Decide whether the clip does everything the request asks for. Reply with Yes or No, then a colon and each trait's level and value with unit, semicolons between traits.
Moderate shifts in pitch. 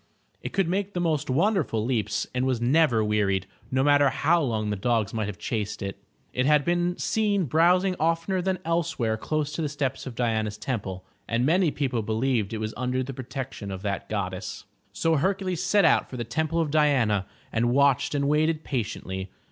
No: wide, 6.7 semitones